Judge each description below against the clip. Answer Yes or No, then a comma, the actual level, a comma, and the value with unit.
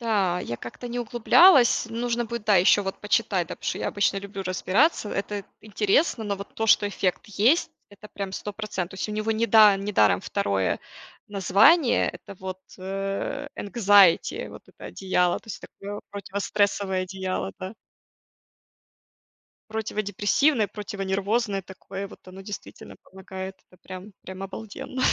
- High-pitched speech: Yes, high, 200 Hz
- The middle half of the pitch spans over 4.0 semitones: No, narrow, 2.4 semitones